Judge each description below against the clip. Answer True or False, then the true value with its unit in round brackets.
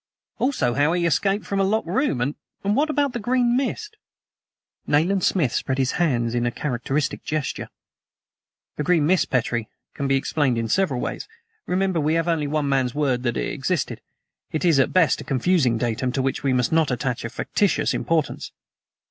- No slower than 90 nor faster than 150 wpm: False (185 wpm)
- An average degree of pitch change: False (6.3 semitones)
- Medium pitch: True (150 Hz)